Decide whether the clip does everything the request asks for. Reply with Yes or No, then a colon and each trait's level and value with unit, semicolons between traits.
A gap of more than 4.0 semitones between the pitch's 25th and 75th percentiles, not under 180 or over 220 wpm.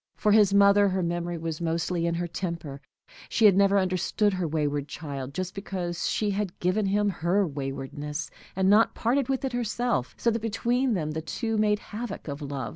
Yes: average, 4.4 semitones; average, 195 wpm